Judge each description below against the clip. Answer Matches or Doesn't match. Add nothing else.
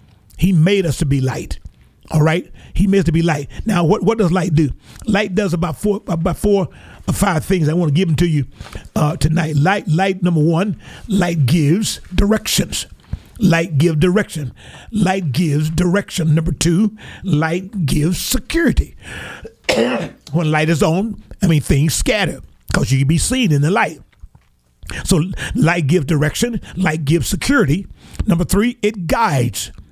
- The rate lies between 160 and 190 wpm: Matches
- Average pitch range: Matches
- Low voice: Doesn't match